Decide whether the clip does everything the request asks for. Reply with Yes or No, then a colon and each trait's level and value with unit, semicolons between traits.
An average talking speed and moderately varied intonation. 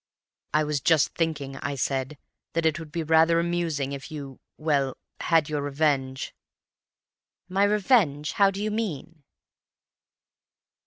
No: slow, 125 wpm; average, 3.1 semitones